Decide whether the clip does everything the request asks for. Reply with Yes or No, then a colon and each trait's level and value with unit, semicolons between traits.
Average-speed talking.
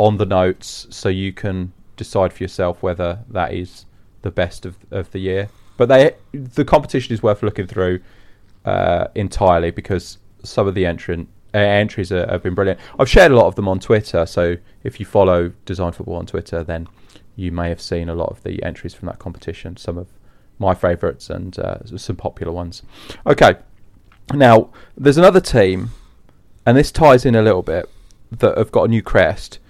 Yes: average, 190 wpm